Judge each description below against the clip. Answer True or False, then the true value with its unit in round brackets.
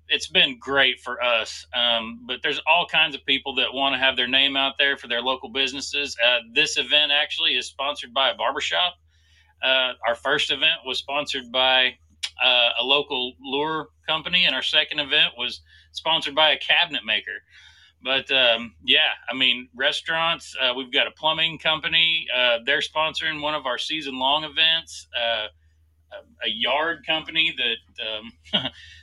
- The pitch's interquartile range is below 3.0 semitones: False (4.3 semitones)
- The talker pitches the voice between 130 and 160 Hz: True (135 Hz)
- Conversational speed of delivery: True (170 wpm)